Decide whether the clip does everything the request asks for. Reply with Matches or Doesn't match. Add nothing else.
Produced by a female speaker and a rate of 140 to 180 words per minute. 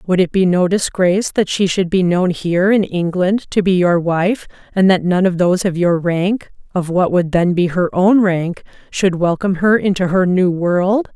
Doesn't match